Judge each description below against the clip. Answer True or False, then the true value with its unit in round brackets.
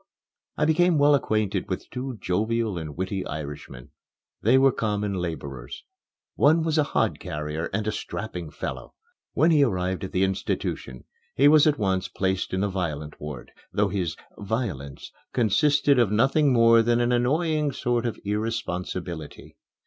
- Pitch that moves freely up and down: True (6.7 semitones)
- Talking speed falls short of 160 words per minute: True (150 wpm)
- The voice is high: False (105 Hz)